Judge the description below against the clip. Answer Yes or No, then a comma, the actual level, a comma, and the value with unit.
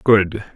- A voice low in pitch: Yes, low, 100 Hz